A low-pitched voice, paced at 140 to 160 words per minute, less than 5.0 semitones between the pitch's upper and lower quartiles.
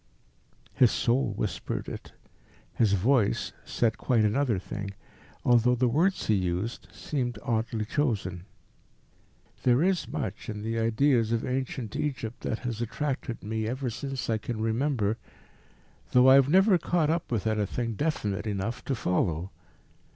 Yes: low, 115 Hz; average, 145 wpm; average, 3.6 semitones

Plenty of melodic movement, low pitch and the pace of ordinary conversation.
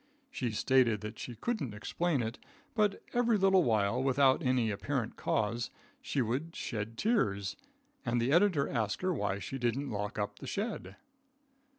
Yes: wide, 7.1 semitones; low, 125 Hz; average, 160 wpm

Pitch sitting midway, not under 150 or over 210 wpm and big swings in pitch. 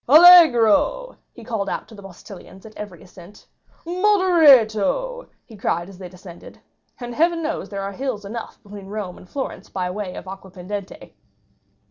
No: high, 210 Hz; average, 160 wpm; wide, 7.8 semitones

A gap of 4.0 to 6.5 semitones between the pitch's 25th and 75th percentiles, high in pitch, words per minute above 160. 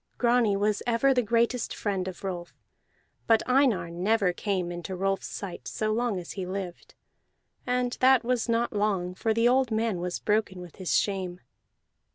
Yes: average, 4.3 semitones; high, 210 Hz; average, 170 wpm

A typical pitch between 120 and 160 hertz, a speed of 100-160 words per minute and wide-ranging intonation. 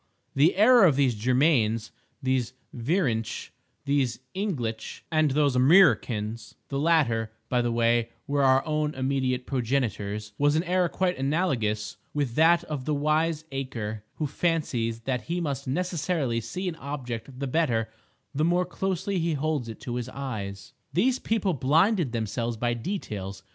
Yes: low, 135 Hz; average, 150 wpm; wide, 5.7 semitones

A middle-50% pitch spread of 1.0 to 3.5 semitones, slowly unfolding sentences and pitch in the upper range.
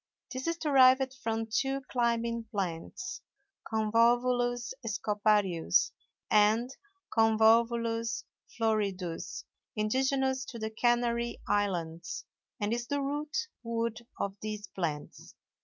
Yes: average, 2.8 semitones; slow, 95 wpm; high, 230 Hz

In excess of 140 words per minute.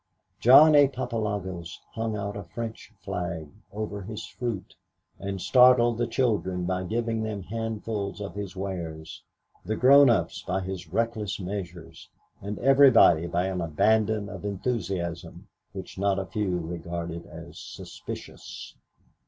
No: slow, 135 wpm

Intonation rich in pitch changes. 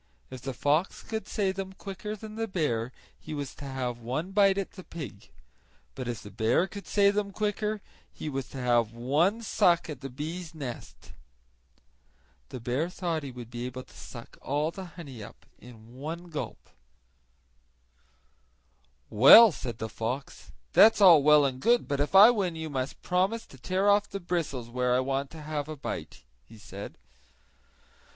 Yes: wide, 7.1 semitones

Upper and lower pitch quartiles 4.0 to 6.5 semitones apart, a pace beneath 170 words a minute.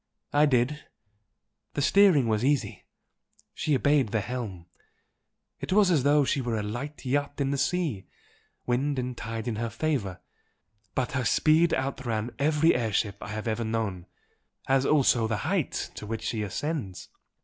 Yes: average, 4.6 semitones; average, 160 wpm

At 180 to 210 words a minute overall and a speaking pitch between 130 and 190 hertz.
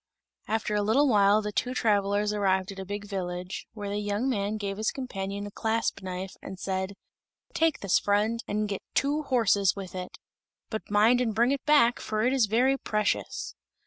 No: average, 190 wpm; high, 210 Hz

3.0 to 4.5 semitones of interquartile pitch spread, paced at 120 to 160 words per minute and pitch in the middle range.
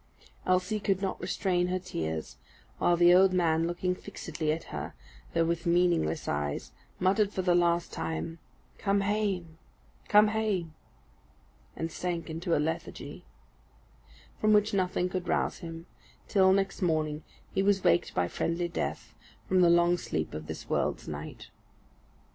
No: narrow, 2.6 semitones; average, 150 wpm; medium, 175 Hz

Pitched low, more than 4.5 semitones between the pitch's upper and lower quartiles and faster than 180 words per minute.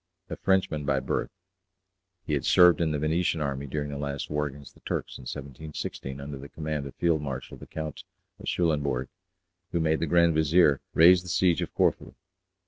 No: very low, 75 Hz; average, 2.9 semitones; average, 190 wpm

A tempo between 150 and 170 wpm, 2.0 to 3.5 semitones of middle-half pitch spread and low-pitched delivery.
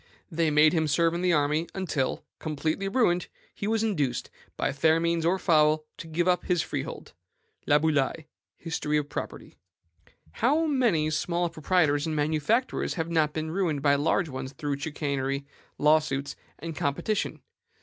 No: average, 155 wpm; average, 2.9 semitones; medium, 160 Hz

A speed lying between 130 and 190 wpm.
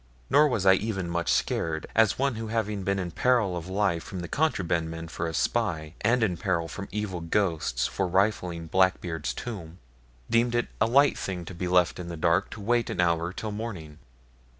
No: average, 200 wpm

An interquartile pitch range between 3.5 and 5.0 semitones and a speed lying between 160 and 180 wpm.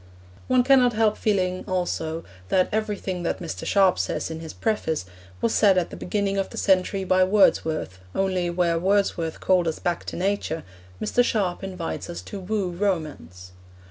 No: average, 2.9 semitones; average, 170 wpm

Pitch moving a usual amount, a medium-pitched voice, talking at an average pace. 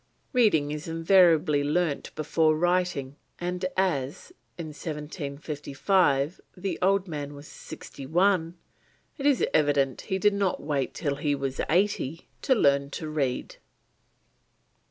No: average, 4.1 semitones; medium, 155 Hz; slow, 125 wpm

